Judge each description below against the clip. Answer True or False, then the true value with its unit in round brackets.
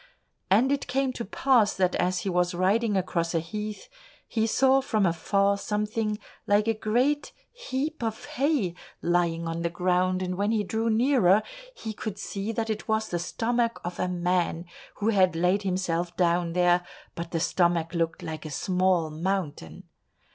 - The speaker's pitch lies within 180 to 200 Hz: True (190 Hz)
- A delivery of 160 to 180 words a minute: True (170 wpm)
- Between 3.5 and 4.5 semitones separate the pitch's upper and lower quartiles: True (4.1 semitones)